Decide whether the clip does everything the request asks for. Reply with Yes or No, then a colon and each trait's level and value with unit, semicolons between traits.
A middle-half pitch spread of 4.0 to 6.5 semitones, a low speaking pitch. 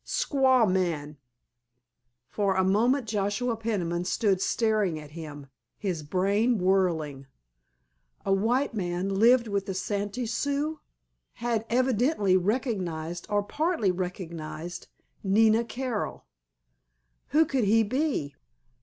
No: average, 4.6 semitones; high, 205 Hz